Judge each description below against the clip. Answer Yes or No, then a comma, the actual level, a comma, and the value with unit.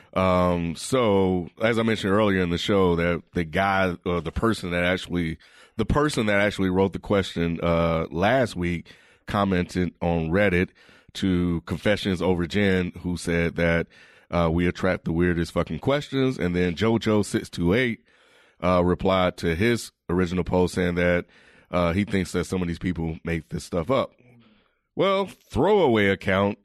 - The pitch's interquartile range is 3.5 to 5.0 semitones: No, narrow, 2.6 semitones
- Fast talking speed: No, average, 165 wpm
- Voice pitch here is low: Yes, very low, 90 Hz